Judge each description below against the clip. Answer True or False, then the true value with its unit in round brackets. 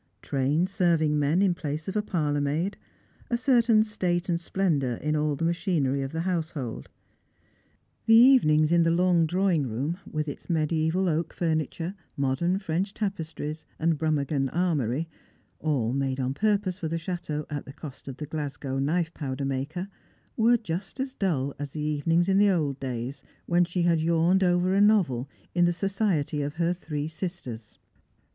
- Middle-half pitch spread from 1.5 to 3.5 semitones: False (4.0 semitones)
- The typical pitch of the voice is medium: True (165 Hz)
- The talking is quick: False (170 wpm)